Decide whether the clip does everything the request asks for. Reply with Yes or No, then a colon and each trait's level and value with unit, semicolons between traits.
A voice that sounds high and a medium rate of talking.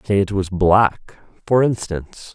No: low, 100 Hz; average, 155 wpm